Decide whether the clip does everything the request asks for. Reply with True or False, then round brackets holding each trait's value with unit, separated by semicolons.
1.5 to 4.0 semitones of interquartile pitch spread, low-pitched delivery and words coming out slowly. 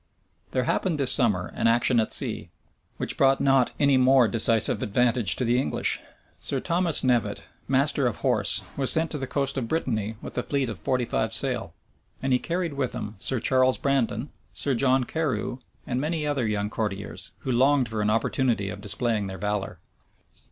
False (3.6 semitones; 125 Hz; 185 wpm)